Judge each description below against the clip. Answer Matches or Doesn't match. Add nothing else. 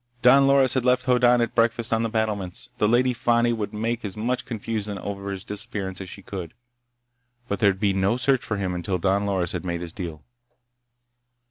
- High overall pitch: Doesn't match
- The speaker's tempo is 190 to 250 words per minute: Matches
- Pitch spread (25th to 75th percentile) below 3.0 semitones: Doesn't match